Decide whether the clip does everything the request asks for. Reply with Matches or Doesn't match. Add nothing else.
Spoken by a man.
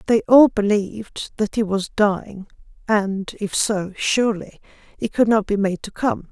Doesn't match